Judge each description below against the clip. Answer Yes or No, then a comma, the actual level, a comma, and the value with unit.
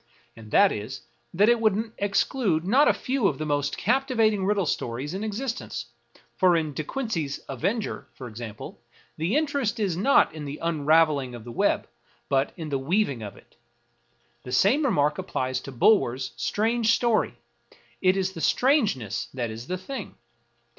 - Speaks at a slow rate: No, average, 175 wpm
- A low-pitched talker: No, medium, 175 Hz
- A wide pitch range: Yes, wide, 8.4 semitones